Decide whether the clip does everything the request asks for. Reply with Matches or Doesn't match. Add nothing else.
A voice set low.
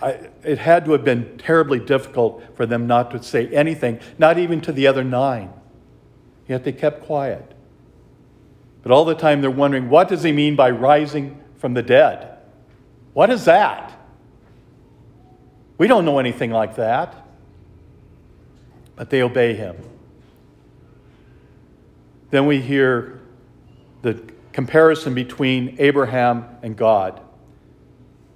Matches